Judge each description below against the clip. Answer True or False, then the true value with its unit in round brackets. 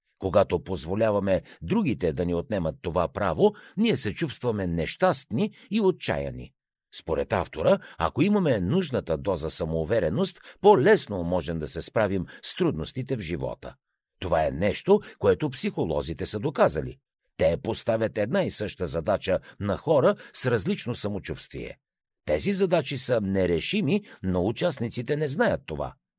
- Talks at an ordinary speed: True (130 wpm)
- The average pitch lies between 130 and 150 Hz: False (120 Hz)